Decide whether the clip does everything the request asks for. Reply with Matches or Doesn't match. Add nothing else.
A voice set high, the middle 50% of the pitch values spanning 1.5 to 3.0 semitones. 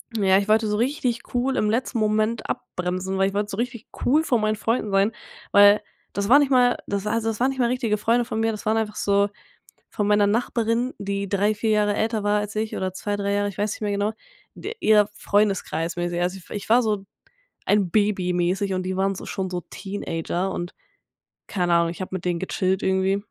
Matches